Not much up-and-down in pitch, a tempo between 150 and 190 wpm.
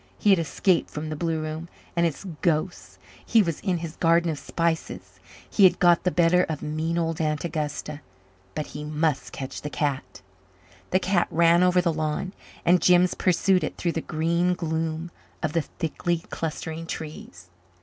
Yes: narrow, 2.0 semitones; average, 175 wpm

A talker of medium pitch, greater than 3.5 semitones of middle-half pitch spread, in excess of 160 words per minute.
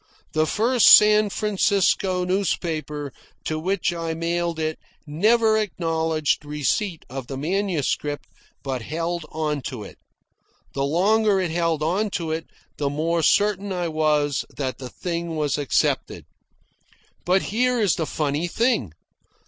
No: medium, 165 Hz; average, 4.5 semitones; slow, 135 wpm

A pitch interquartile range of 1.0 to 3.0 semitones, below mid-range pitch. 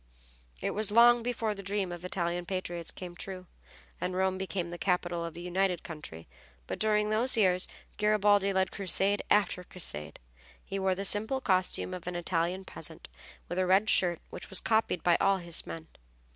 No: average, 2.7 semitones; medium, 185 Hz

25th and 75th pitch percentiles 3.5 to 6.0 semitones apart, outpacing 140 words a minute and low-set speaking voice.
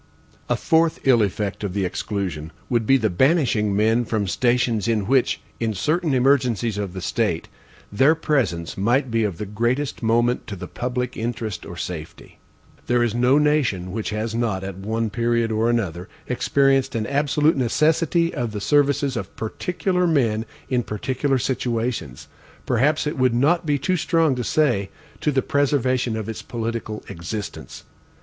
Yes: average, 4.4 semitones; average, 165 wpm; low, 120 Hz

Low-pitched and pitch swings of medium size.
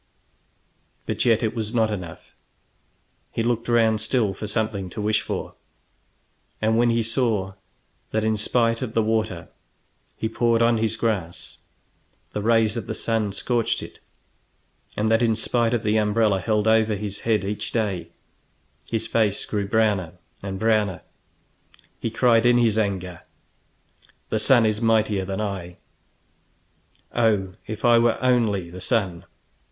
No: low, 110 Hz; narrow, 2.0 semitones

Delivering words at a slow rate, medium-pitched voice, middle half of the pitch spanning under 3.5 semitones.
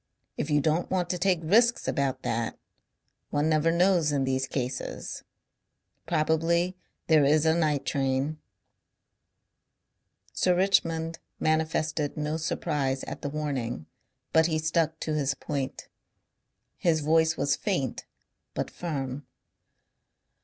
Yes: slow, 120 wpm; medium, 155 Hz; average, 2.8 semitones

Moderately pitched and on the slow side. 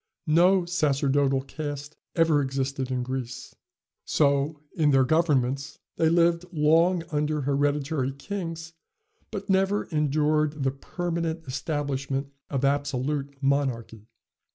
Yes: medium, 145 Hz; slow, 105 wpm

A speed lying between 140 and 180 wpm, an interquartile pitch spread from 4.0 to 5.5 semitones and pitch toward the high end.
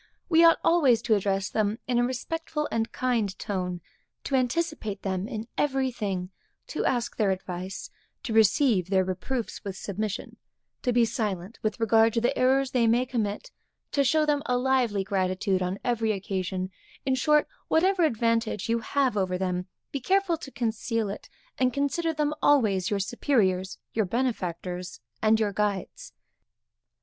Yes: average, 160 wpm; average, 5.2 semitones; high, 225 Hz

